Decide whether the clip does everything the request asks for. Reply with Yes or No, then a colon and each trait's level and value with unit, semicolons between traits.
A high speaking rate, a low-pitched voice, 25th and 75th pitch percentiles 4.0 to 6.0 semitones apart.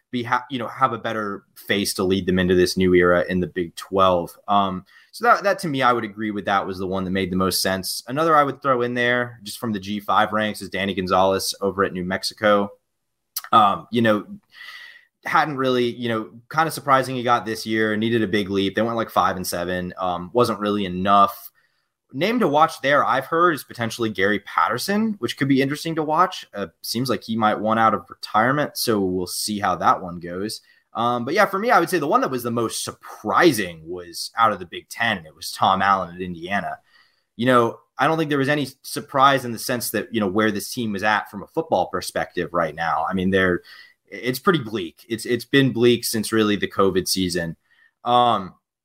Yes: fast, 225 wpm; low, 110 Hz; average, 4.3 semitones